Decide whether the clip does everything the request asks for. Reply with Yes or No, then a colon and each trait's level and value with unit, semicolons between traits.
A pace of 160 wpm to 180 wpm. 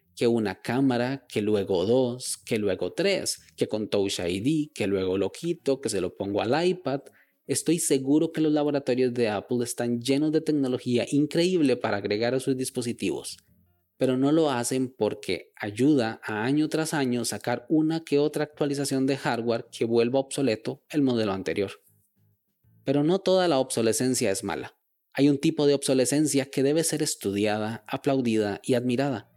Yes: average, 170 wpm